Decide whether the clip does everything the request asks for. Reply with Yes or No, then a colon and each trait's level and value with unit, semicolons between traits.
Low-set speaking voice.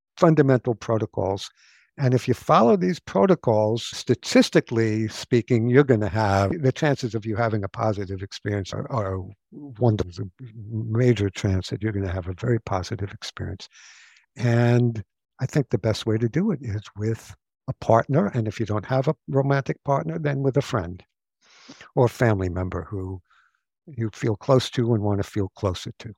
Yes: low, 115 Hz